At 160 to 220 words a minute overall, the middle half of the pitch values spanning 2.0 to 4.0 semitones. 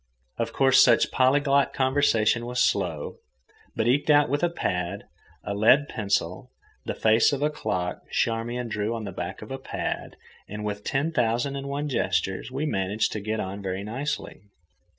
No: average, 170 wpm; wide, 5.4 semitones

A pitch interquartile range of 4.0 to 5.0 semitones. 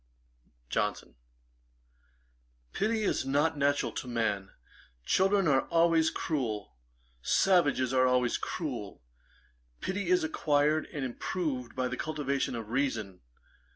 Yes: average, 4.6 semitones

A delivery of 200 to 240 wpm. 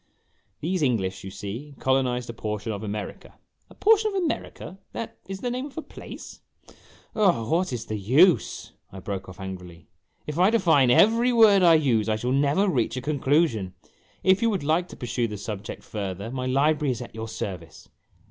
Yes: fast, 205 wpm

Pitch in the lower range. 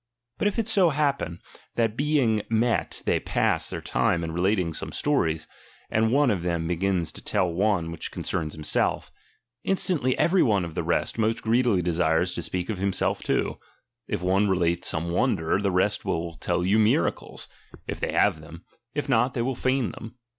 Yes: low, 100 Hz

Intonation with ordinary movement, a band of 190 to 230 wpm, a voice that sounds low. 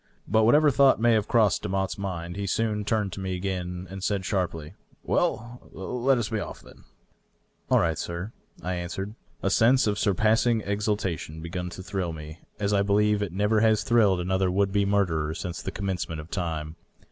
Yes: average, 3.2 semitones; average, 195 wpm; low, 100 Hz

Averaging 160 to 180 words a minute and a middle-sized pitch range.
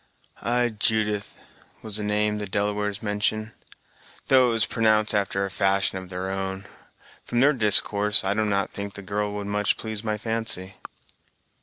No: average, 165 wpm; narrow, 1.6 semitones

